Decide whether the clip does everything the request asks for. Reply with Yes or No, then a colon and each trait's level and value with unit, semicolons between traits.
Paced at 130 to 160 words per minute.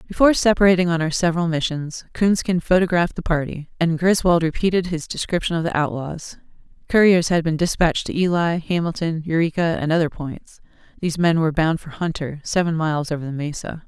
No: average, 175 wpm